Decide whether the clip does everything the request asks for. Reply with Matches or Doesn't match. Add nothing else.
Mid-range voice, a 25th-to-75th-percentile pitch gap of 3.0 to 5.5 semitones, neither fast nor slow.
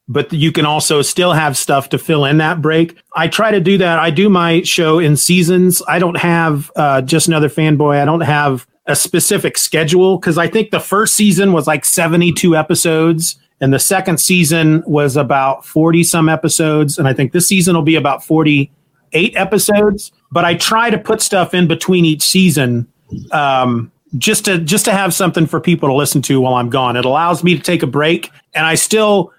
Doesn't match